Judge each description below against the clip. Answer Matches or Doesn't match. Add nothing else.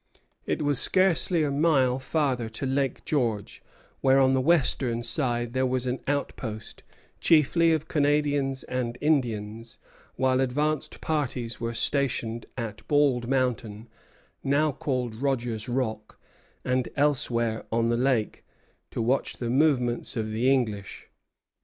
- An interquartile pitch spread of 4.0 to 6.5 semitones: Doesn't match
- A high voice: Doesn't match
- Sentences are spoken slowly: Matches